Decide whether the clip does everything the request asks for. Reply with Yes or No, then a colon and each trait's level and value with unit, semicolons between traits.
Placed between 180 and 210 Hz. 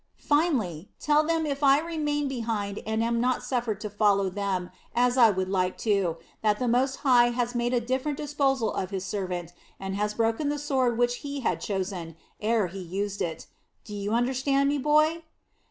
No: high, 235 Hz